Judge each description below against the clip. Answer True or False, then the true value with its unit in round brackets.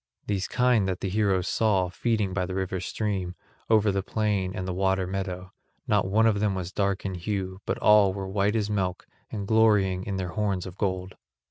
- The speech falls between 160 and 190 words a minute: False (200 wpm)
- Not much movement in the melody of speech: True (2.0 semitones)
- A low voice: True (95 Hz)